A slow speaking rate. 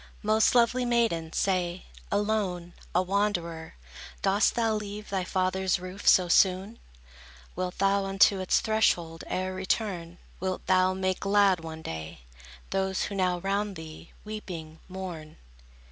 Yes: slow, 130 wpm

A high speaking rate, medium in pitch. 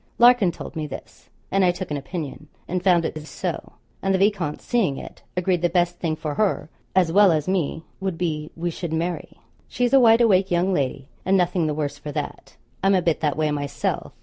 Yes: fast, 225 wpm; medium, 175 Hz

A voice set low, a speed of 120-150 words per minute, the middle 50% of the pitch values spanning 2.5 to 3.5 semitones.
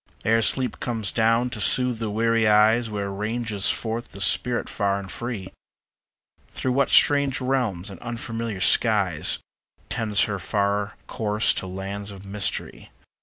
Yes: low, 110 Hz; average, 145 wpm; average, 2.8 semitones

